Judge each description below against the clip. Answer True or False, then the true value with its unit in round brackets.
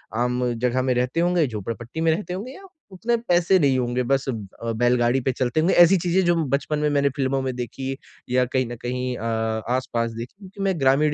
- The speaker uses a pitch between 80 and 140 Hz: True (135 Hz)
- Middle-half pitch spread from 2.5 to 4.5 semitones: False (5.2 semitones)